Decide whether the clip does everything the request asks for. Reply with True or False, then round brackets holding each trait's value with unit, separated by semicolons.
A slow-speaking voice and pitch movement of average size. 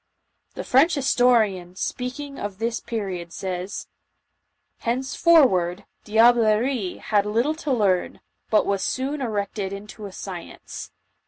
True (115 wpm; 4.8 semitones)